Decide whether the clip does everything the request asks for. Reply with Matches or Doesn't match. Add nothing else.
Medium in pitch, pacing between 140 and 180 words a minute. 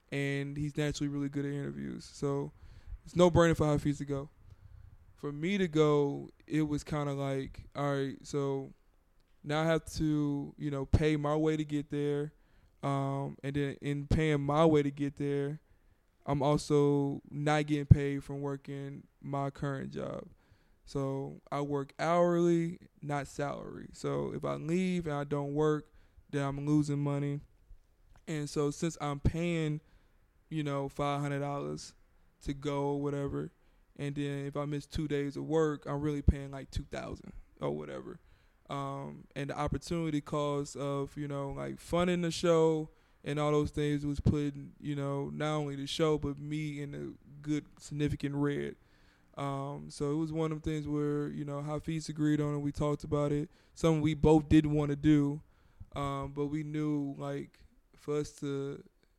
Matches